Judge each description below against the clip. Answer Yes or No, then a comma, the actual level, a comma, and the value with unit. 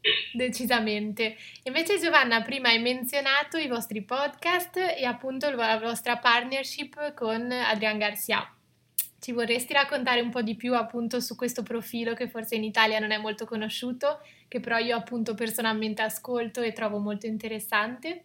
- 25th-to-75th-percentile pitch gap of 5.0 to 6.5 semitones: No, average, 2.8 semitones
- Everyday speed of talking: Yes, average, 150 wpm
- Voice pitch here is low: No, high, 235 Hz